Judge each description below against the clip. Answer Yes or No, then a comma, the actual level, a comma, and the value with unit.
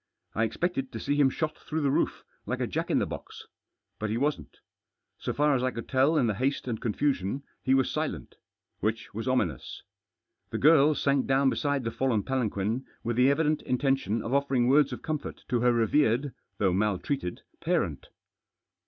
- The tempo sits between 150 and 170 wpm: No, average, 185 wpm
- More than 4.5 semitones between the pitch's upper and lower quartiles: No, average, 3.8 semitones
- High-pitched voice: No, low, 130 Hz